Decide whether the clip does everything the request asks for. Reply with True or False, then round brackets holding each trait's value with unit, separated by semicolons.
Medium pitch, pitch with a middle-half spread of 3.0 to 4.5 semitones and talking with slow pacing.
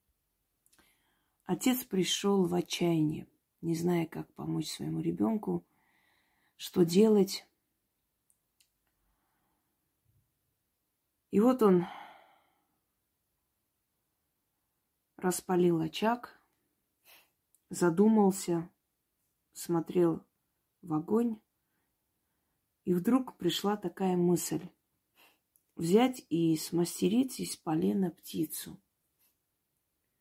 True (180 Hz; 3.3 semitones; 65 wpm)